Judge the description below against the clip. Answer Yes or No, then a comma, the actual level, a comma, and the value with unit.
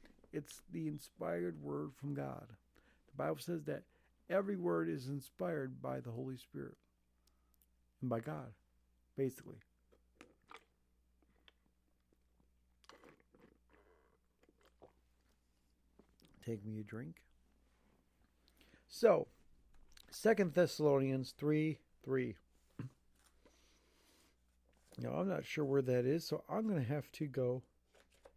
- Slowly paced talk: Yes, slow, 95 wpm